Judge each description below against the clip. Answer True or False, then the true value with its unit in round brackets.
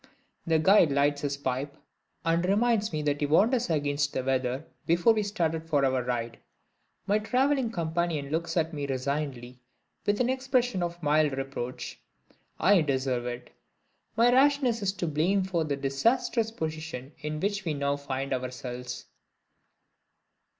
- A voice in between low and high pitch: True (155 Hz)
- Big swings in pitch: True (6.5 semitones)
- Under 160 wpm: True (150 wpm)